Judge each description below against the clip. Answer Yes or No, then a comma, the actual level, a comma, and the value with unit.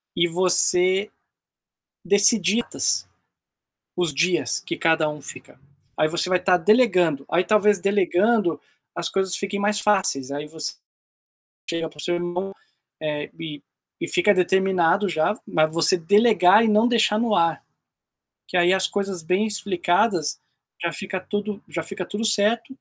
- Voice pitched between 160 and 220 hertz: Yes, medium, 185 Hz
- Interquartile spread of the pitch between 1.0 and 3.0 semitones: No, average, 3.7 semitones